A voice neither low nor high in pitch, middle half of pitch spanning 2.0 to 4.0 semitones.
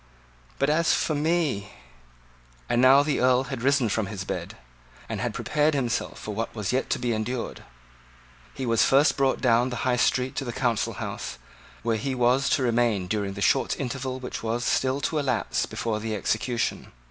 No: low, 125 Hz; average, 3.4 semitones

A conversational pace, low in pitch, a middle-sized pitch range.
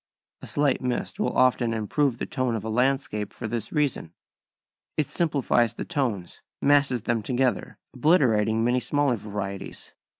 Yes: average, 145 wpm; low, 125 Hz; average, 4.1 semitones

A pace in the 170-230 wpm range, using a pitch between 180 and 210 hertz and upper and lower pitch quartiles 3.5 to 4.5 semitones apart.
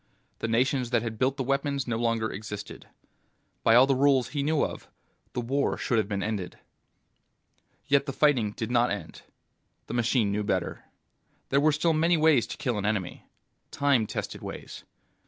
No: average, 175 wpm; low, 125 Hz; average, 3.9 semitones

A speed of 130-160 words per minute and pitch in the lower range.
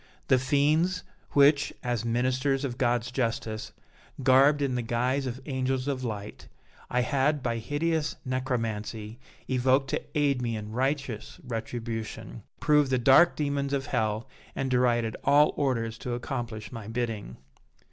Yes: average, 140 wpm; low, 130 Hz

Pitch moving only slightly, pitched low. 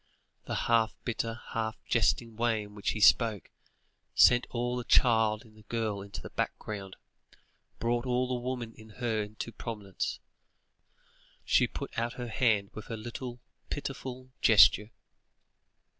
Yes: narrow, 2.1 semitones; low, 115 Hz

